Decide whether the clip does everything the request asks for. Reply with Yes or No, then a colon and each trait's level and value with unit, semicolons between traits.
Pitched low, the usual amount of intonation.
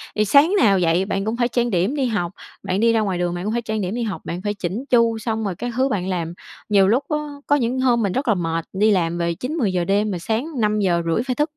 No: high, 210 Hz; average, 4.6 semitones